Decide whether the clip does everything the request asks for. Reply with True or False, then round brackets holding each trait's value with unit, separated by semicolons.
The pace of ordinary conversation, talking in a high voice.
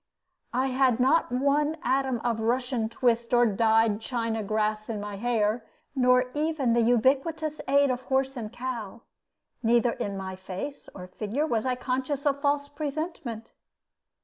True (150 wpm; 245 Hz)